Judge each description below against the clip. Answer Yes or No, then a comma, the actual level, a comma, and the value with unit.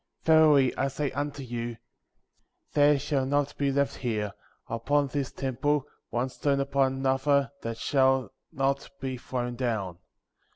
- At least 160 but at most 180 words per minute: No, slow, 135 wpm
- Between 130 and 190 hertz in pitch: Yes, low, 135 Hz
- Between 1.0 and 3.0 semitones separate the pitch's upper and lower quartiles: Yes, narrow, 2.4 semitones